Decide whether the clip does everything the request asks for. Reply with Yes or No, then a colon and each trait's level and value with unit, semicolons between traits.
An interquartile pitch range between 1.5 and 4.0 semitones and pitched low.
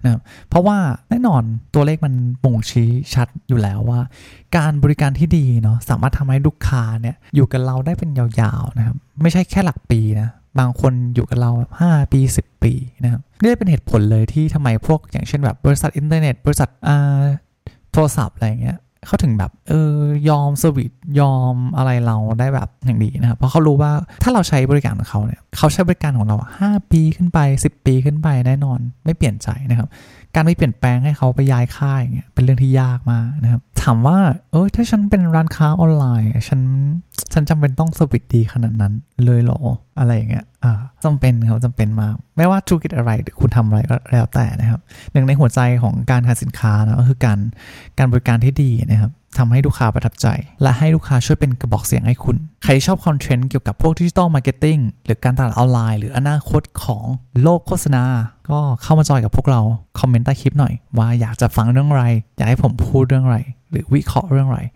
Yes: average, 3.7 semitones; low, 130 Hz